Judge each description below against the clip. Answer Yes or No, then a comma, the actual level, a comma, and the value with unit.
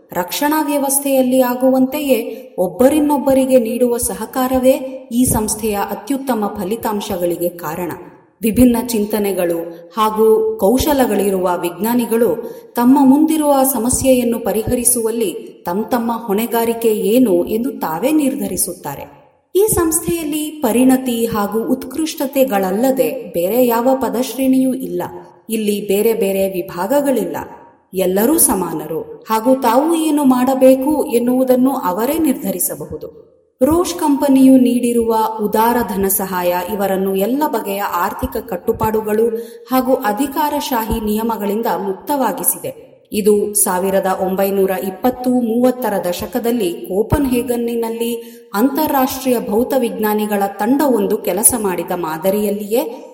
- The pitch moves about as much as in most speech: Yes, average, 4.1 semitones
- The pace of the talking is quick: No, average, 90 wpm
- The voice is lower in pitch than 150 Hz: No, high, 235 Hz